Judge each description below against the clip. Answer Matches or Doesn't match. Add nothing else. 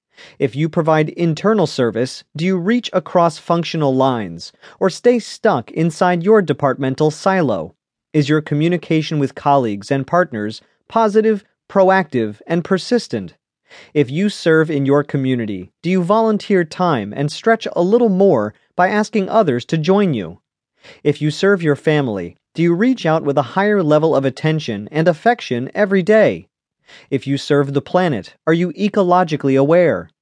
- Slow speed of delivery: Doesn't match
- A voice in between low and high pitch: Matches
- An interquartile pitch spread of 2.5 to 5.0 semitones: Doesn't match